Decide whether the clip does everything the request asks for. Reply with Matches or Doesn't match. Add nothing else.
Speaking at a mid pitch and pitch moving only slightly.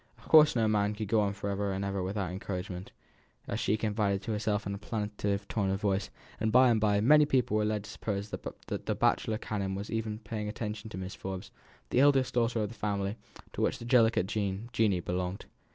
Doesn't match